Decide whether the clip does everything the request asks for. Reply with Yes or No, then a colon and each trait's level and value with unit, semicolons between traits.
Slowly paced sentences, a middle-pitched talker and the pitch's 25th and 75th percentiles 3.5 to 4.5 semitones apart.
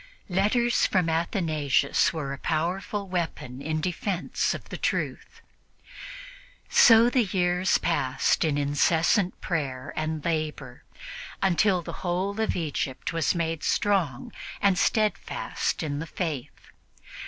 Yes: slow, 115 wpm; medium, 170 Hz; average, 4.1 semitones